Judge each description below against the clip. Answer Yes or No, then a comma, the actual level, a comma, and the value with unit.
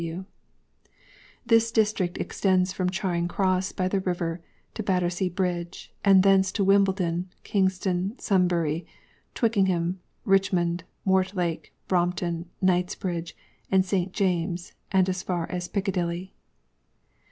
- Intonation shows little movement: Yes, narrow, 1.6 semitones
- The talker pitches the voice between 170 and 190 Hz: Yes, medium, 185 Hz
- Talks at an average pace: No, slow, 105 wpm